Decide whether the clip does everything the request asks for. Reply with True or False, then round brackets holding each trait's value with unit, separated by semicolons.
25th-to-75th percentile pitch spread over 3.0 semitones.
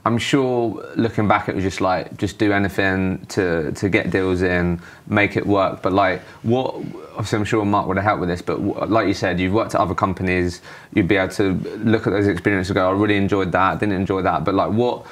False (2.5 semitones)